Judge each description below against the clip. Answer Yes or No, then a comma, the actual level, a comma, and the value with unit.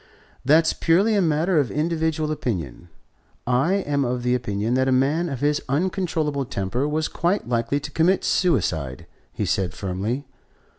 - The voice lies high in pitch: No, medium, 145 Hz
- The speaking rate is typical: Yes, average, 155 wpm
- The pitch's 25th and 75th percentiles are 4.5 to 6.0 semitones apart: Yes, average, 5.0 semitones